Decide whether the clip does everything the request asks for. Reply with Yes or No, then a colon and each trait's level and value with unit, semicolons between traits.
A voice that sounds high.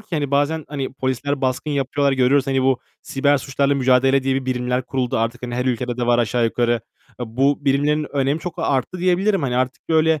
No: low, 135 Hz